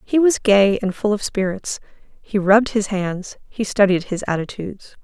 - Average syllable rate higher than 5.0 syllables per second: No, 4.6 syllables/s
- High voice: Yes, high, 200 Hz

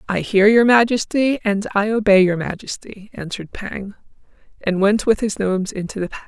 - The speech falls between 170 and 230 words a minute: Yes, average, 180 wpm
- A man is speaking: No, female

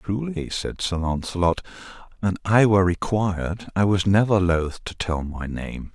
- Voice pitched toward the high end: No, very low, 95 Hz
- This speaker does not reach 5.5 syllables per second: Yes, 4.5 syllables/s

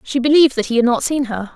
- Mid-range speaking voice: No, very high, 260 Hz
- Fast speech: Yes, fast, 310 wpm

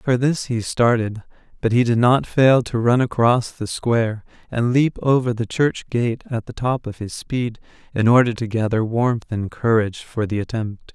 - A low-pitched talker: Yes, low, 120 Hz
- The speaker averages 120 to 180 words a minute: No, average, 195 wpm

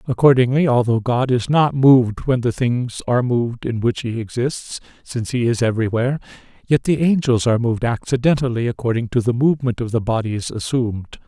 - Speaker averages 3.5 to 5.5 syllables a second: No, 5.8 syllables/s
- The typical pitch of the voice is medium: No, low, 125 Hz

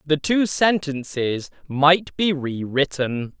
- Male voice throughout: Yes, male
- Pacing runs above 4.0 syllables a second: No, 3.2 syllables/s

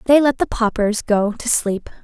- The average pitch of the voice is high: Yes, high, 225 Hz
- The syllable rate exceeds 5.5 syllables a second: No, 4.6 syllables/s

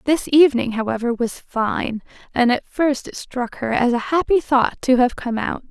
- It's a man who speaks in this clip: No, female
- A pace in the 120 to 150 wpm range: No, average, 200 wpm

